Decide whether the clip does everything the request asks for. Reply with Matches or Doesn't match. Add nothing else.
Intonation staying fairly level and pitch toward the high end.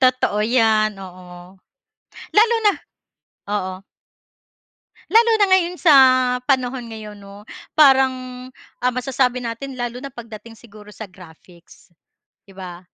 Doesn't match